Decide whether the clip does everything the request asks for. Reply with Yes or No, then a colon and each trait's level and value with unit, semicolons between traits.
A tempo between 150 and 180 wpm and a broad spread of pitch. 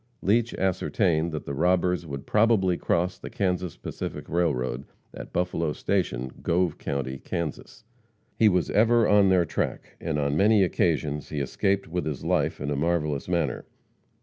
No: average, 155 wpm; average, 4.2 semitones